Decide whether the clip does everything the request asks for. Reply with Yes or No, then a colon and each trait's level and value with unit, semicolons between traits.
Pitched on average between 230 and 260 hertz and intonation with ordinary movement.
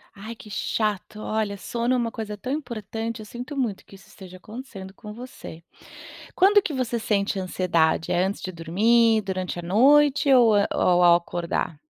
No: high, 210 Hz; average, 4.2 semitones